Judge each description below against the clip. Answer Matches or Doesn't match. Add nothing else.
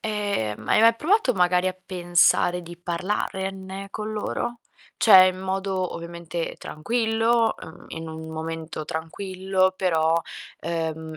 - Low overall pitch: Doesn't match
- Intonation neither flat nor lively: Matches